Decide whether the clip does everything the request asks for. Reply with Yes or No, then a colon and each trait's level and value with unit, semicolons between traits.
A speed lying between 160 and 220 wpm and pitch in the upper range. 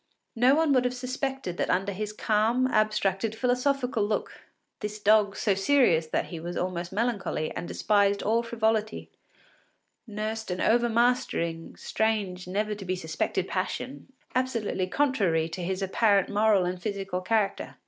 No: average, 145 wpm; high, 210 Hz